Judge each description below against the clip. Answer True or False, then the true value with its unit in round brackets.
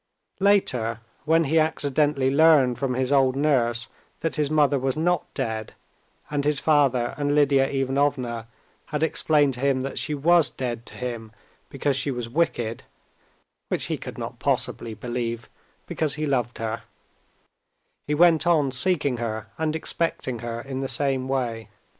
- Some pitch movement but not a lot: True (3.6 semitones)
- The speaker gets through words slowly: False (155 wpm)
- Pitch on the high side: False (135 Hz)